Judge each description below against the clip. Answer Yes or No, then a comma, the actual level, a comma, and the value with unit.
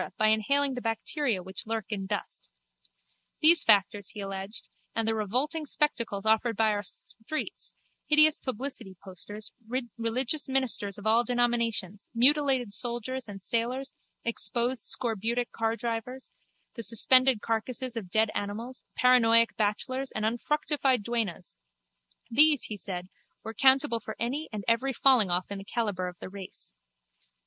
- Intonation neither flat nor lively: Yes, average, 3.9 semitones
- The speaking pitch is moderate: No, high, 230 Hz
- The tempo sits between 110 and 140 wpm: Yes, slow, 135 wpm